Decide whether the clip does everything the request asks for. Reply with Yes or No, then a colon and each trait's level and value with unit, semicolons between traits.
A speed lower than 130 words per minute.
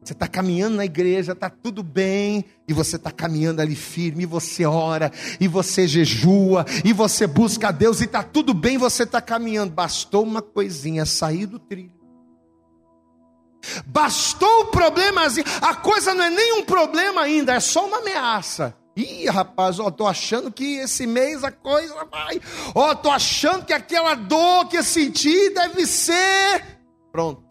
No: average, 165 wpm